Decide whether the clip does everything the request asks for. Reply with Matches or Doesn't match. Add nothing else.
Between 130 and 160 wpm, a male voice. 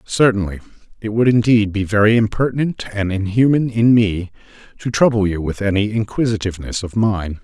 Matches